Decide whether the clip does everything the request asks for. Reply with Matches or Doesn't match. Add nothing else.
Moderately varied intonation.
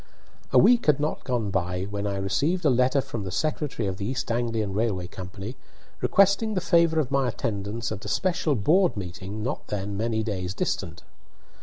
Doesn't match